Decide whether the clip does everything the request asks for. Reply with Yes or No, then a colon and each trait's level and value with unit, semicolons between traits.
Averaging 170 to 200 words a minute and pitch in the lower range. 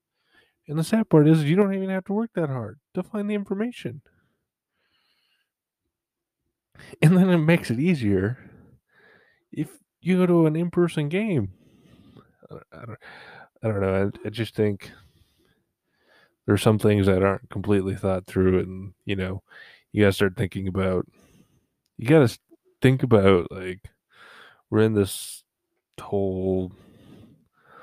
No: average, 150 wpm; low, 110 Hz